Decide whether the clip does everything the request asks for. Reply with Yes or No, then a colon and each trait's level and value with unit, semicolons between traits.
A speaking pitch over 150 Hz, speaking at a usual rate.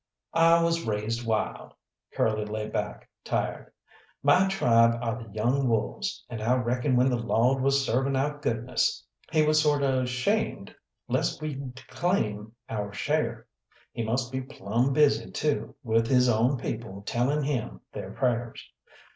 No: low, 125 Hz; average, 150 wpm